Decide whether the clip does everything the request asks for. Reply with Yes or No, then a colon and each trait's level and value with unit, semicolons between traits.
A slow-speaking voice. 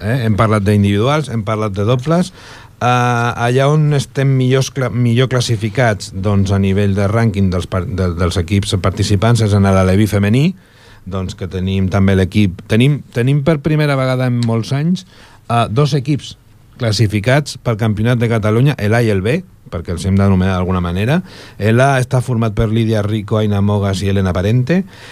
No: fast, 170 wpm